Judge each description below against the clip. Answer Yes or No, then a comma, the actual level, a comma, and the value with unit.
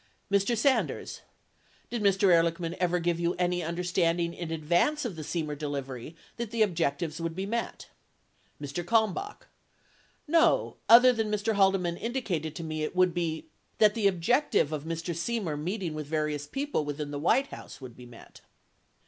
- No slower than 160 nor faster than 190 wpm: Yes, average, 170 wpm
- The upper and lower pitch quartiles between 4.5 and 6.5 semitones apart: Yes, average, 5.1 semitones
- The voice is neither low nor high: Yes, medium, 175 Hz